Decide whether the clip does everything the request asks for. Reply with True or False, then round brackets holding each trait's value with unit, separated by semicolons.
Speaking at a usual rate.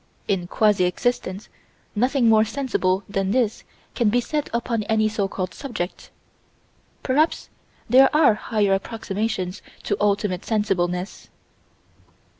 False (120 wpm)